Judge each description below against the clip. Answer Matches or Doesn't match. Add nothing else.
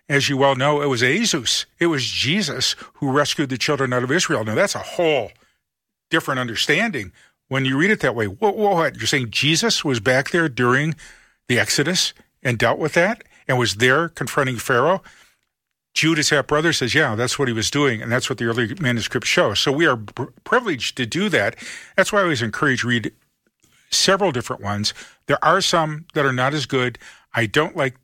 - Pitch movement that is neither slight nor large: Matches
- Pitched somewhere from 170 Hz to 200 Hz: Doesn't match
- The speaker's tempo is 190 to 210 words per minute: Matches